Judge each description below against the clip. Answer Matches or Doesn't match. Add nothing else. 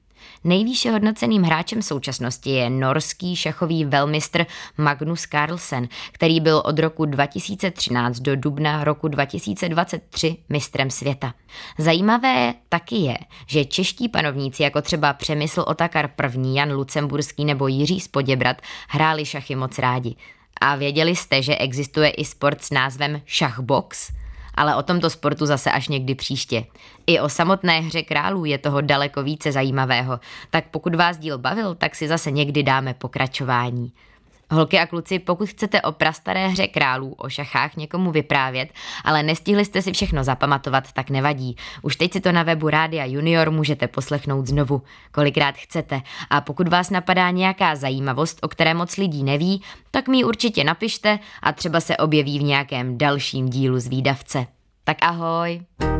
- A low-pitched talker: Doesn't match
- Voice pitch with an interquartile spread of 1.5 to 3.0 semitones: Doesn't match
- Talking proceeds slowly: Doesn't match